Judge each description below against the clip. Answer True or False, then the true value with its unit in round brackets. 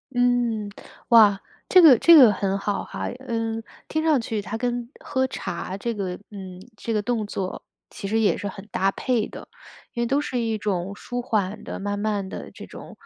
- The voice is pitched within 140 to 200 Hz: False (215 Hz)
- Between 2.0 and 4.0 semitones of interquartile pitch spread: True (3.5 semitones)